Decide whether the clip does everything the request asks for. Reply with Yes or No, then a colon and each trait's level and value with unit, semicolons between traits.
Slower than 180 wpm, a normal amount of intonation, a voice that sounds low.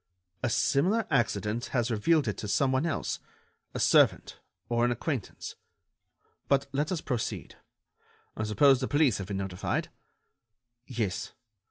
Yes: average, 140 wpm; average, 4.8 semitones; low, 120 Hz